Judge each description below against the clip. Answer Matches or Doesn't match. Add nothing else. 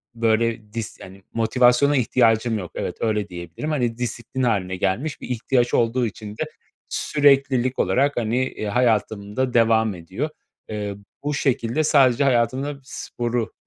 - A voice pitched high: Doesn't match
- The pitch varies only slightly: Doesn't match